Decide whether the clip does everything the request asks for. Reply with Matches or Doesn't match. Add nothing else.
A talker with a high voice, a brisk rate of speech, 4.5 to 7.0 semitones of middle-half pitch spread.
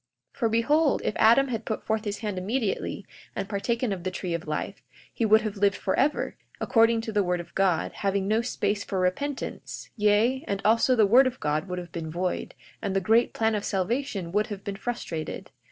Doesn't match